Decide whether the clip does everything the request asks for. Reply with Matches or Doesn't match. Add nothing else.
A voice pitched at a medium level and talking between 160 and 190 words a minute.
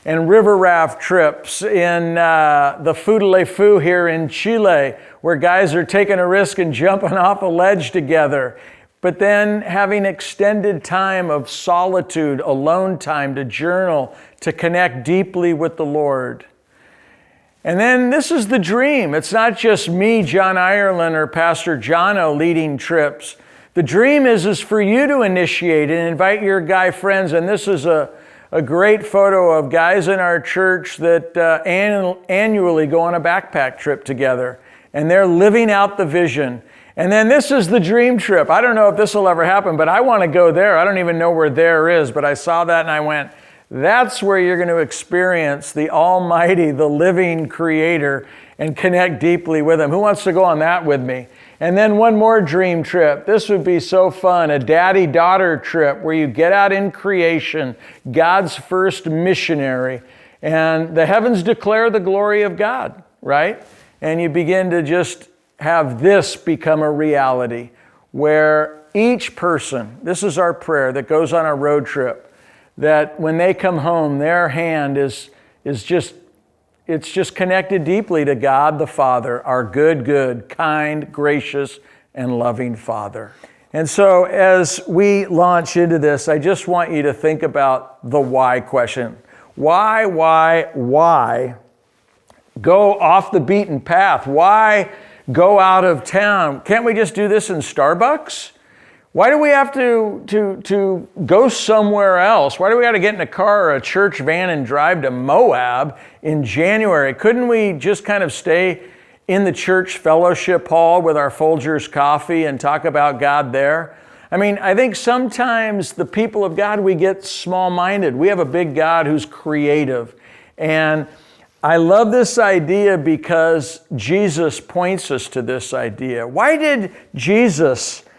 Matches